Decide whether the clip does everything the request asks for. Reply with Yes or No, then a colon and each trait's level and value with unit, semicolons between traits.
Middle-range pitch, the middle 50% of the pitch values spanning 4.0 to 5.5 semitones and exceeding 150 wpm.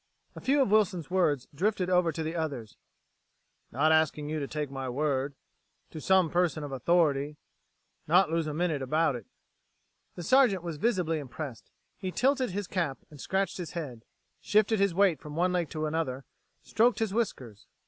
Yes: medium, 165 Hz; average, 4.4 semitones; average, 175 wpm